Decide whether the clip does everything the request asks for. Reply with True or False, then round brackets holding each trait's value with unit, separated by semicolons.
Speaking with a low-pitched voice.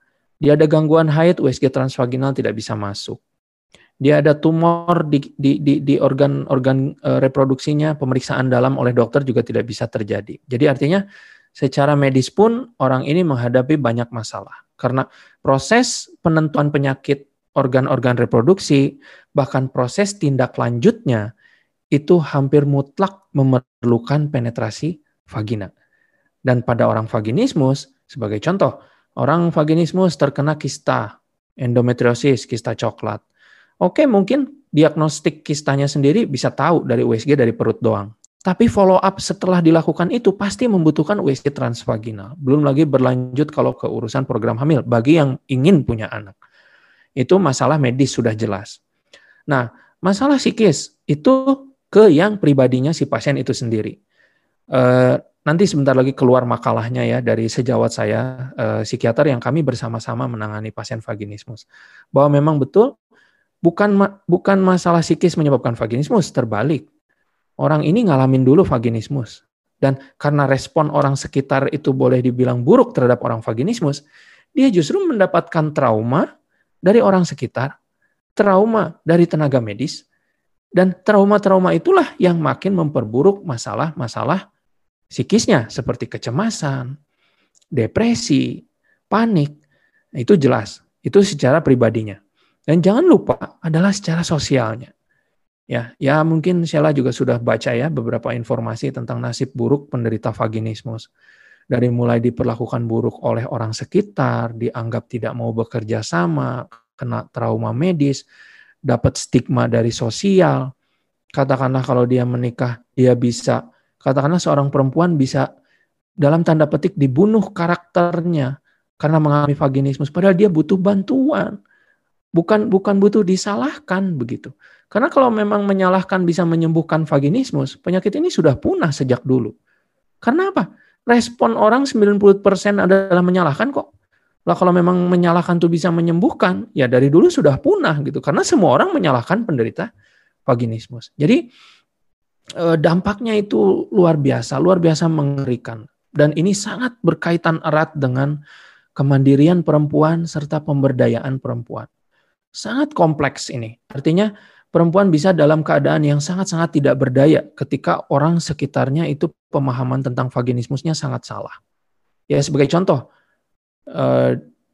False (145 Hz)